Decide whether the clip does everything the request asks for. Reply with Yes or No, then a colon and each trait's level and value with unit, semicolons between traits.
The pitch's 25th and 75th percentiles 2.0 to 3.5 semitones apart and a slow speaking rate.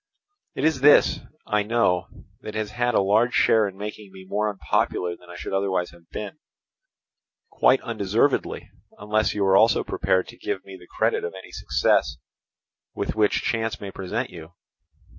No: average, 2.8 semitones; average, 165 wpm